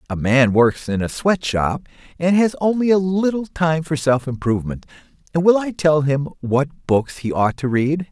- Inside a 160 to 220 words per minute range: Yes, average, 190 wpm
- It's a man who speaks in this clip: Yes, male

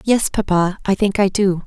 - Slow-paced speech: No, fast, 215 wpm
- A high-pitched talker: Yes, high, 195 Hz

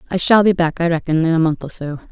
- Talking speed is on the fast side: Yes, fast, 310 wpm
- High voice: No, medium, 170 Hz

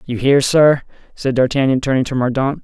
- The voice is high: No, low, 135 Hz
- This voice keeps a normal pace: Yes, average, 180 wpm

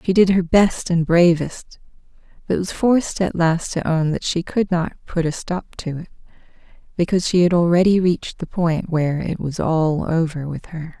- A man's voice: No, female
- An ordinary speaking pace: Yes, average, 195 wpm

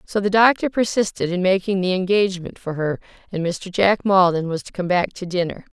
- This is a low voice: No, medium, 185 Hz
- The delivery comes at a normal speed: No, fast, 210 wpm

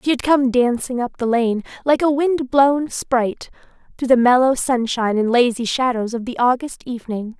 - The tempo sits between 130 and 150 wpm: No, average, 185 wpm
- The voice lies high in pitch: Yes, very high, 250 Hz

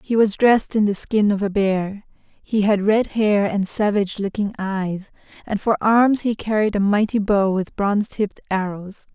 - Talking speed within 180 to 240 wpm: Yes, average, 190 wpm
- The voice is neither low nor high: No, high, 205 Hz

